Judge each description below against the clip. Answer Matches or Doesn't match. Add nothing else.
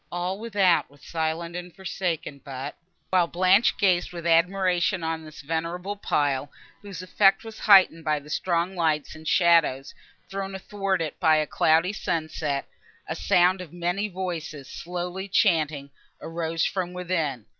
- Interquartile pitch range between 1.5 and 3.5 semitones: Matches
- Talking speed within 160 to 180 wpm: Doesn't match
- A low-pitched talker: Doesn't match